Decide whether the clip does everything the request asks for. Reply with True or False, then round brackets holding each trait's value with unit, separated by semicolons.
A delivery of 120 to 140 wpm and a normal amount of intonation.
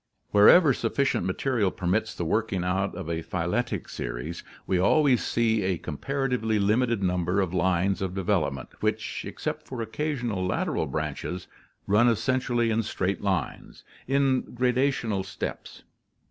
True (135 wpm; 4.8 semitones)